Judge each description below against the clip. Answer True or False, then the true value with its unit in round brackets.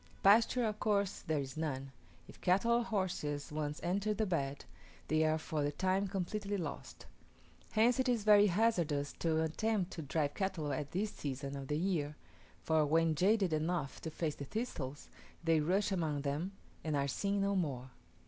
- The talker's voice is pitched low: False (165 Hz)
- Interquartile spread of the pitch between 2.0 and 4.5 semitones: False (5.4 semitones)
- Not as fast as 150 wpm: False (175 wpm)